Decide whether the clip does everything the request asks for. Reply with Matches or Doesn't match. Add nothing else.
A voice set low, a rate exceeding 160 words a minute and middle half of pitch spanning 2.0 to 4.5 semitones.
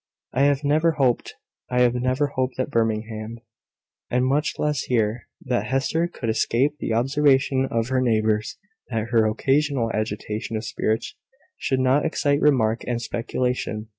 Doesn't match